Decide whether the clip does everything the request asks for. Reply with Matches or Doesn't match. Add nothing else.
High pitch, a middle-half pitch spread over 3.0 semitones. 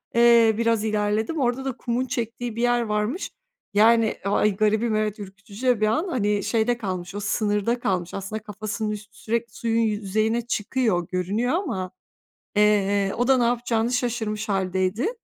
Doesn't match